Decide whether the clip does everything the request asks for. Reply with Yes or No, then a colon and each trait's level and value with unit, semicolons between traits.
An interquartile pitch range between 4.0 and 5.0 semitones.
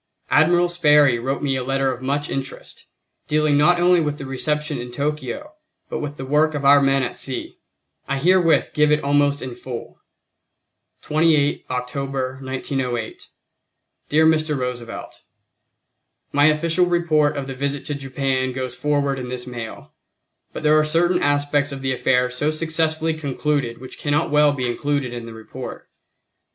No: average, 2.7 semitones